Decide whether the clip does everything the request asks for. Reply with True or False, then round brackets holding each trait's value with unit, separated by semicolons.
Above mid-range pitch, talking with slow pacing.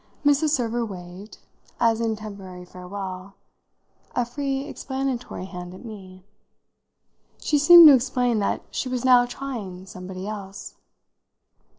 True (220 Hz; 120 wpm)